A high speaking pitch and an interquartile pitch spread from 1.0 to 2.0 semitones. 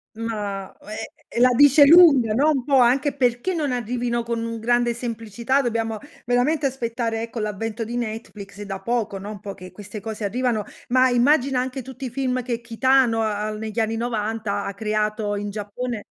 No: high, 230 Hz; average, 2.8 semitones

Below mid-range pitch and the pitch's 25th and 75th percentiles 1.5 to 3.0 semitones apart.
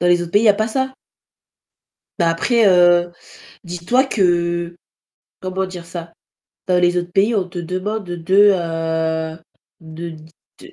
No: medium, 175 Hz; narrow, 2.4 semitones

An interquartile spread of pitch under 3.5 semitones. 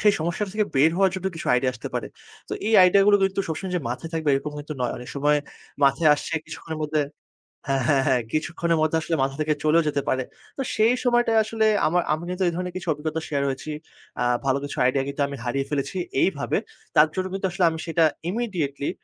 No: average, 5.0 semitones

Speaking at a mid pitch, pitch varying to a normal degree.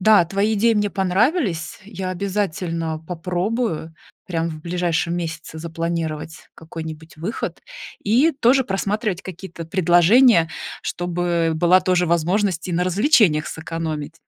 Yes: medium, 175 Hz; average, 3.5 semitones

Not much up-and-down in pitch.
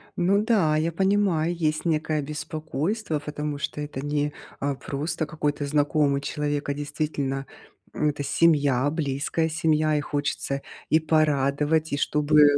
Yes: narrow, 1.5 semitones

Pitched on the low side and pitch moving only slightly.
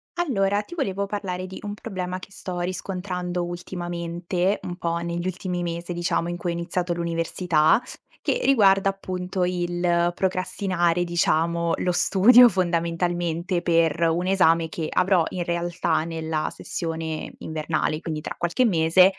No: medium, 175 Hz; narrow, 1.7 semitones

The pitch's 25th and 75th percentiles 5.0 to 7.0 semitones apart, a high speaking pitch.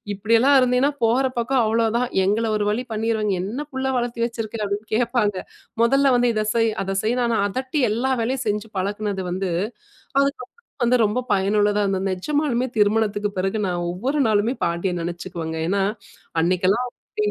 No: average, 3.8 semitones; high, 220 Hz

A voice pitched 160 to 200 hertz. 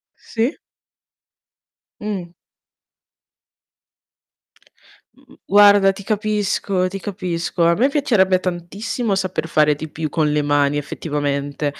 Yes: medium, 185 Hz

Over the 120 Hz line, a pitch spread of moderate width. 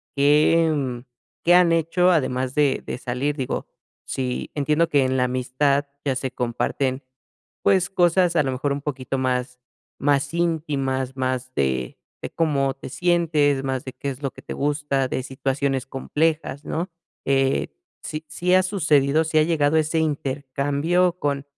Yes: medium, 140 Hz; average, 3.4 semitones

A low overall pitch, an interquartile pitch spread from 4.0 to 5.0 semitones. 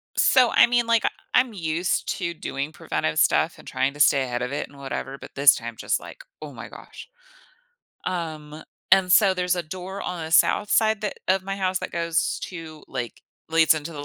No: medium, 165 Hz; average, 4.6 semitones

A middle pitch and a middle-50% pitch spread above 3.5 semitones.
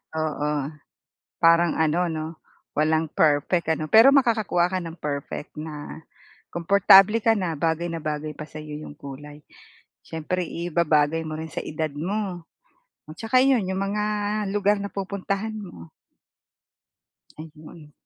Yes: medium, 165 Hz; average, 4.3 semitones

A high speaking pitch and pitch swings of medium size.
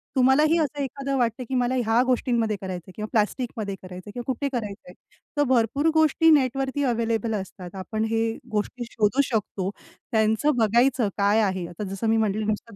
Yes: high, 225 Hz; average, 3.7 semitones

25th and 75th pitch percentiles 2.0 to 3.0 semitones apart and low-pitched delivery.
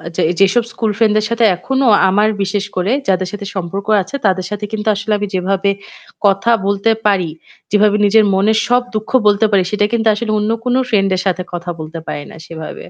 No: narrow, 2.4 semitones; high, 205 Hz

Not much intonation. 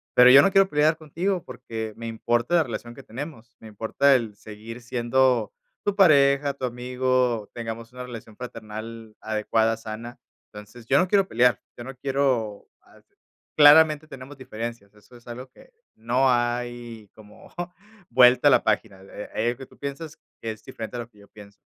No: average, 3.3 semitones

